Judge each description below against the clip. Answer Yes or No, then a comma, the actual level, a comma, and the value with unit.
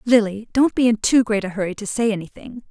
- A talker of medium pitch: No, high, 220 Hz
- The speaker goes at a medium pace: No, fast, 245 wpm